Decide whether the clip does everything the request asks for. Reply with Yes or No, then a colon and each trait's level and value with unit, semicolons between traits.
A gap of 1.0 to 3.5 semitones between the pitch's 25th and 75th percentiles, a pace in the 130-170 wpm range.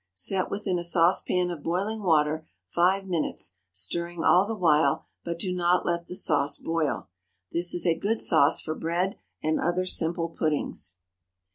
Yes: narrow, 2.4 semitones; average, 160 wpm